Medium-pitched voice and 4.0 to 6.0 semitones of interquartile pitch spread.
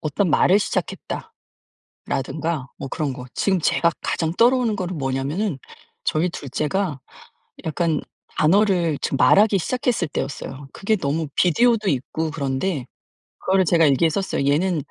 Yes: medium, 165 Hz; average, 5.2 semitones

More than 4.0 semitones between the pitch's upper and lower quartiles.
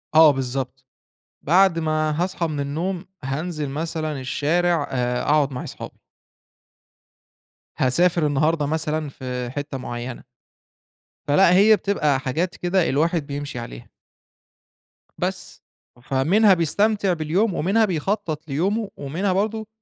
Yes: average, 4.5 semitones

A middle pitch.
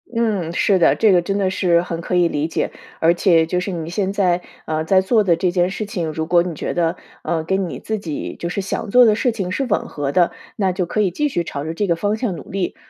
Yes: medium, 180 Hz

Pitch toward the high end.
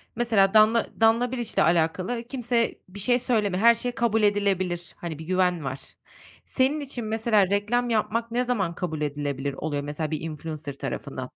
Yes: high, 205 Hz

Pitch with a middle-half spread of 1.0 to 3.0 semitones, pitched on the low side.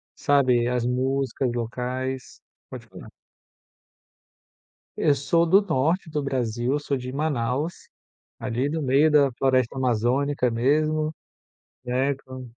Yes: average, 2.7 semitones; low, 130 Hz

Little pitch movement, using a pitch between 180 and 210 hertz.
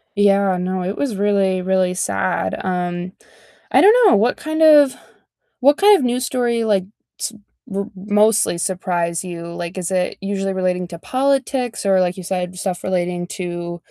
No: average, 4.1 semitones; high, 190 Hz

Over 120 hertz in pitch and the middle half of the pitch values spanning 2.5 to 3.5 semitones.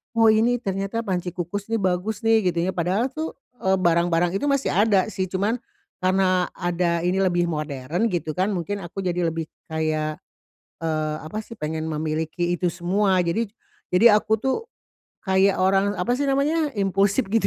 No: medium, 185 Hz; average, 3.9 semitones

